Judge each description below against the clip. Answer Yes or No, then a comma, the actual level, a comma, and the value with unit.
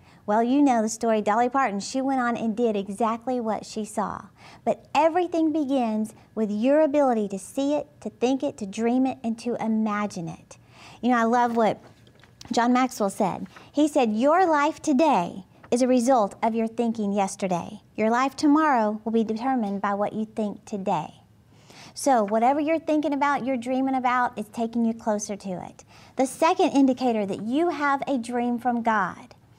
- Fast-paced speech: No, average, 185 wpm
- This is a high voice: Yes, high, 235 Hz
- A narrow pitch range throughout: No, average, 3.8 semitones